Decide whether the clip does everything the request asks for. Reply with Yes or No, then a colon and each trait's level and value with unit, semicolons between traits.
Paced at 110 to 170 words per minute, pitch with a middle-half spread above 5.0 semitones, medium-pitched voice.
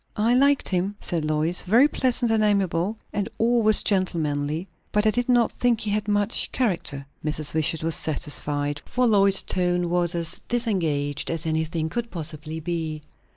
Yes: average, 160 wpm; wide, 5.5 semitones; medium, 180 Hz